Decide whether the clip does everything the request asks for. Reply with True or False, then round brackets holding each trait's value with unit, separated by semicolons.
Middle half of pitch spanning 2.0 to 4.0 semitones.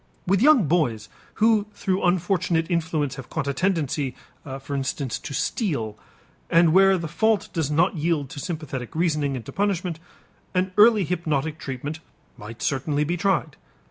False (4.6 semitones)